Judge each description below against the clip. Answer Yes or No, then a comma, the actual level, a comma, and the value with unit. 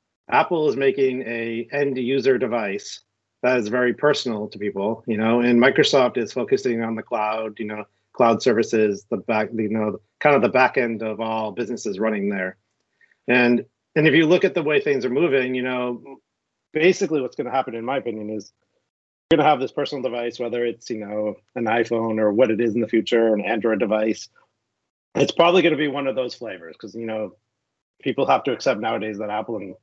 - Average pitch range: Yes, average, 3.2 semitones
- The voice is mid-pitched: No, low, 115 Hz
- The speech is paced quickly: Yes, fast, 210 wpm